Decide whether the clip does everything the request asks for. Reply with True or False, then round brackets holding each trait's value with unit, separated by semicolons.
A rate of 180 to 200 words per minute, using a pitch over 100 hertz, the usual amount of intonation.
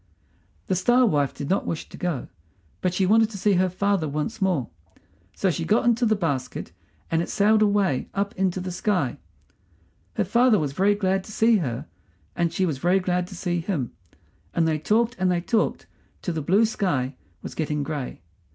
True (195 wpm; 185 Hz; 4.3 semitones)